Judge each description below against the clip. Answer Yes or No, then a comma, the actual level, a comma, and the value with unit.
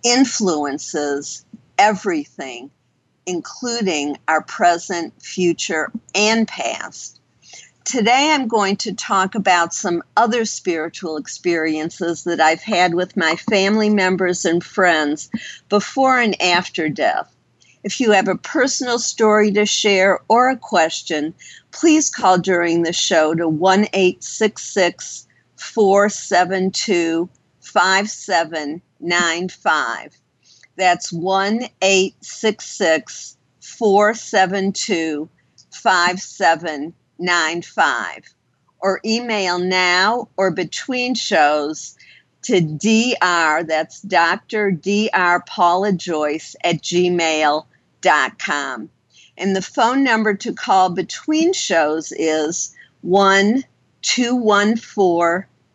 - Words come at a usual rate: No, slow, 100 wpm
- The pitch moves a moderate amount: Yes, average, 4.3 semitones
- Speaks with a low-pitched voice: No, medium, 185 Hz